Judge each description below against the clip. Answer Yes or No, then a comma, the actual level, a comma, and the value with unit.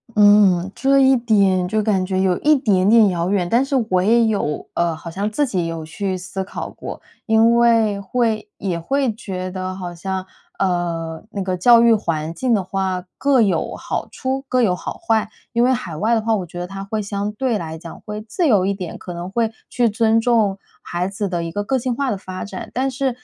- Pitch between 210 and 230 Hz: No, high, 200 Hz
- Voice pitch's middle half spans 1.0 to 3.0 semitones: No, average, 4.1 semitones